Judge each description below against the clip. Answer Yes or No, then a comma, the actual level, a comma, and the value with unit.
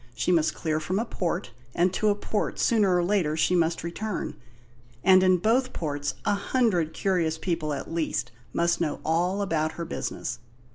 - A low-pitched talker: No, medium, 175 Hz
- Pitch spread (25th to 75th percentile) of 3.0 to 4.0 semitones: Yes, average, 3.5 semitones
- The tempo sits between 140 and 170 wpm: No, average, 180 wpm